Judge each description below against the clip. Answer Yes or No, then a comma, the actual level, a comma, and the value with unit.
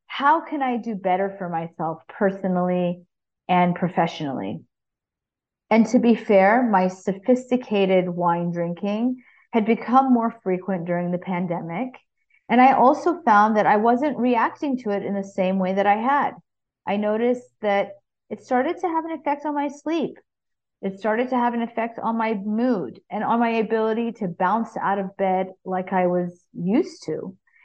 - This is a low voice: No, high, 215 Hz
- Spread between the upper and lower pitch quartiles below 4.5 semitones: No, average, 5.0 semitones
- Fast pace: No, average, 165 wpm